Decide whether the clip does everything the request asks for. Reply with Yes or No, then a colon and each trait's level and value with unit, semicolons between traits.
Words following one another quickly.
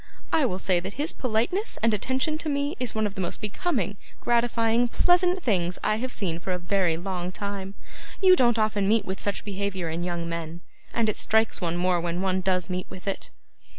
Yes: fast, 210 wpm